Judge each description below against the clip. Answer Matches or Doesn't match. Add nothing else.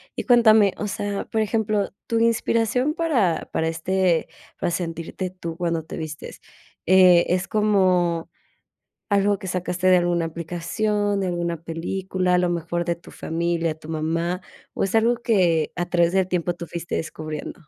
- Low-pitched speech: Doesn't match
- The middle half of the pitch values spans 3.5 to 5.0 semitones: Doesn't match